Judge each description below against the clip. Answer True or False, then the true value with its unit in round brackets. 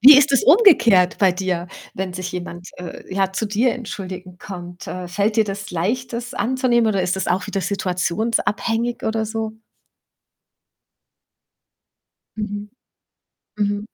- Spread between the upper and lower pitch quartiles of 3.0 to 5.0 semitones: True (3.9 semitones)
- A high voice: True (205 Hz)